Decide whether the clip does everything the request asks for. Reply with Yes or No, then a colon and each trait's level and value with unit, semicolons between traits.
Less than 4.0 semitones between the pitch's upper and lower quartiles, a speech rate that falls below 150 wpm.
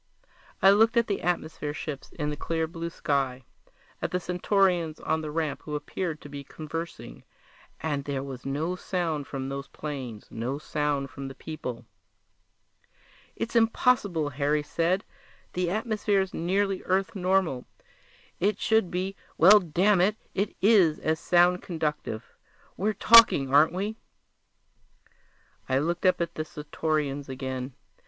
No: average, 4.7 semitones; average, 140 wpm